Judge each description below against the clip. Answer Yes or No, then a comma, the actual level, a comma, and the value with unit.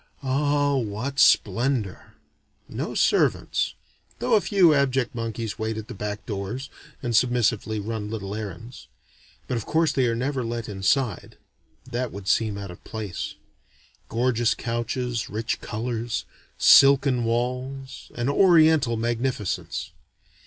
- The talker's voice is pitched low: Yes, low, 120 Hz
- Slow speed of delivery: Yes, slow, 125 wpm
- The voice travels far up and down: No, average, 3.4 semitones